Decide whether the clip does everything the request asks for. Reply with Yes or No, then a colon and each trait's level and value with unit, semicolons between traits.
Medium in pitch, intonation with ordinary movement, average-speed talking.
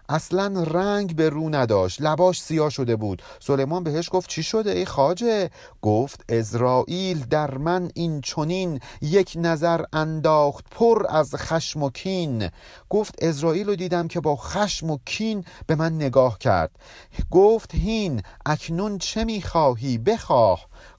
Yes: medium, 160 Hz; average, 4.7 semitones; average, 140 wpm